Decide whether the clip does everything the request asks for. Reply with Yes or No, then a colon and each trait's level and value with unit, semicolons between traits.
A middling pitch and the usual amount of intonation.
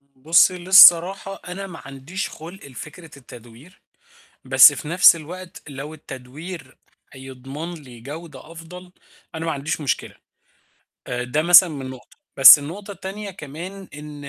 Yes: medium, 160 Hz; average, 4.7 semitones